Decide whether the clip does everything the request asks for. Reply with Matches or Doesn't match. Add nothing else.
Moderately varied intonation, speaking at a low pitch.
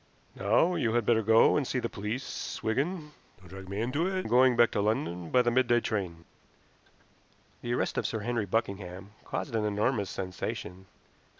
Matches